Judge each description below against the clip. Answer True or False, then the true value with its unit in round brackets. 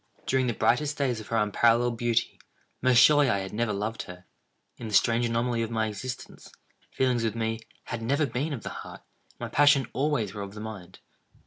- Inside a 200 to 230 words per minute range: True (205 wpm)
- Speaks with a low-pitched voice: True (115 Hz)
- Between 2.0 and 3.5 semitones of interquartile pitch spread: True (2.7 semitones)